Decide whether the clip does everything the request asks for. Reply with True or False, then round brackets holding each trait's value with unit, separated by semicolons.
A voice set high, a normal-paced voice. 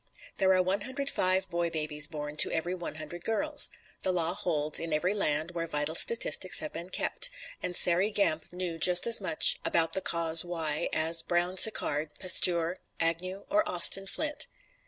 False (175 Hz; 175 wpm)